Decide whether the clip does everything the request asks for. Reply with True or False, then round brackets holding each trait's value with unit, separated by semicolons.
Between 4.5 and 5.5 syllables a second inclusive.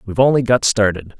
False (6.6 syllables/s)